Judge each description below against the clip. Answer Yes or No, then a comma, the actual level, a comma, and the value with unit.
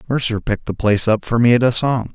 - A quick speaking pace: Yes, fast, 280 wpm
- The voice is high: No, low, 115 Hz